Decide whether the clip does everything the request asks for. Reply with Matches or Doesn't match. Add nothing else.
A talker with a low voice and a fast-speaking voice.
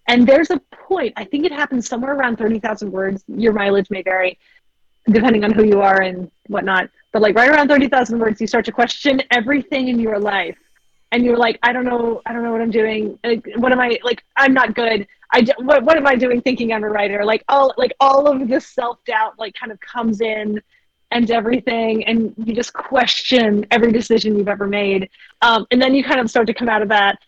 Doesn't match